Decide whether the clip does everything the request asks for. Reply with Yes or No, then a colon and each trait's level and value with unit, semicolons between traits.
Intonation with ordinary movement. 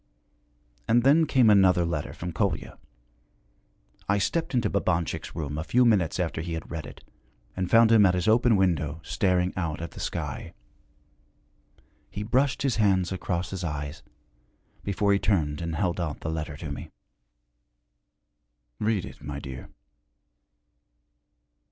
Yes: average, 4.7 semitones